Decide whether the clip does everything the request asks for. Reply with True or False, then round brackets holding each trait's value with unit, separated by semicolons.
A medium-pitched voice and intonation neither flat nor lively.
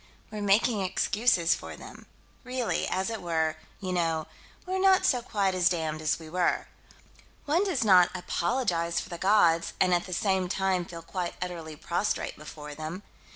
True (180 Hz; 3.7 semitones)